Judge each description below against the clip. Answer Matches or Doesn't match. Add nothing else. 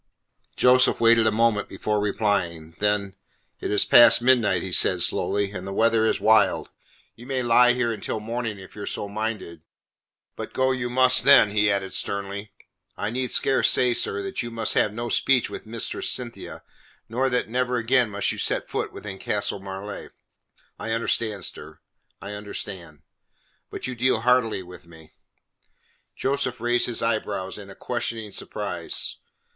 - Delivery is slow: Doesn't match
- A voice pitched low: Matches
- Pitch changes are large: Doesn't match